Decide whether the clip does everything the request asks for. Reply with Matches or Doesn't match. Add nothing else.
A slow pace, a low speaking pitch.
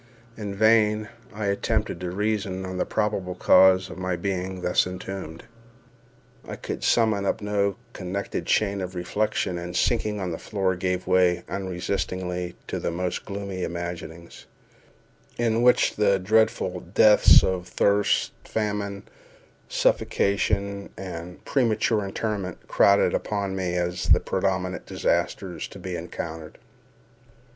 Matches